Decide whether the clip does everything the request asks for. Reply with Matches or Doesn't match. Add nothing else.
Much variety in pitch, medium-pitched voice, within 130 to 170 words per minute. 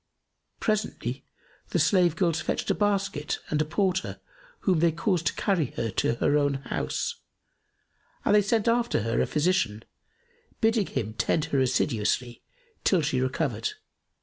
Matches